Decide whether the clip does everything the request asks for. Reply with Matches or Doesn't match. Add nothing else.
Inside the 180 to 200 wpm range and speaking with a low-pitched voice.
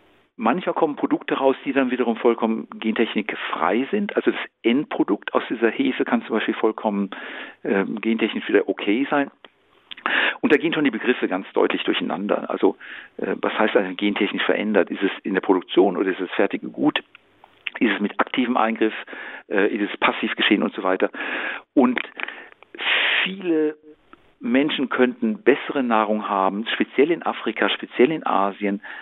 Doesn't match